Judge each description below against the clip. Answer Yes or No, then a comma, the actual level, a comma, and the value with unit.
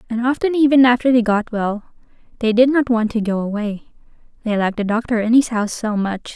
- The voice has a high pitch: Yes, high, 230 Hz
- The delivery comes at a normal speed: No, fast, 210 wpm